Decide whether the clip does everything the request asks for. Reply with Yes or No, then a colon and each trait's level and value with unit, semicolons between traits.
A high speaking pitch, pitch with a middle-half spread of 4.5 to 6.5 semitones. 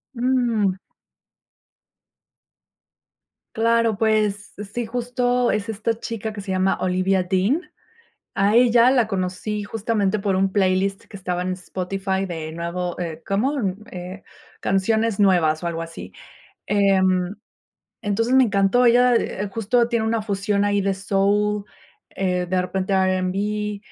No: high, 200 Hz; average, 3.0 semitones